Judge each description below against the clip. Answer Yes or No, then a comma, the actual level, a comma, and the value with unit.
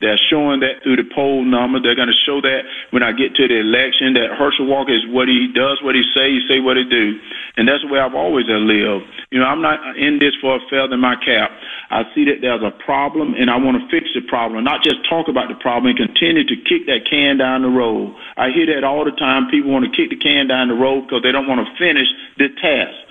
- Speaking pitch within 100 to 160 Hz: Yes, low, 135 Hz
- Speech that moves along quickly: Yes, fast, 265 wpm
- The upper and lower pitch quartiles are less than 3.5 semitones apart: Yes, average, 2.7 semitones